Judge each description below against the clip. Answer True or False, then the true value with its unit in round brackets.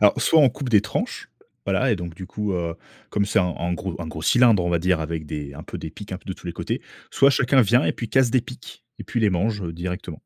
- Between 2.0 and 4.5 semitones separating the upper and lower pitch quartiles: False (5.3 semitones)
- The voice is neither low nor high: False (95 Hz)